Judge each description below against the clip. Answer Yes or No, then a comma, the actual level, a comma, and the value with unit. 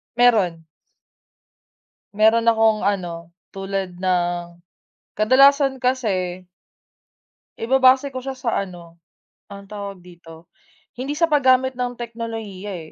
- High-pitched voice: Yes, high, 215 Hz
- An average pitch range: No, wide, 5.7 semitones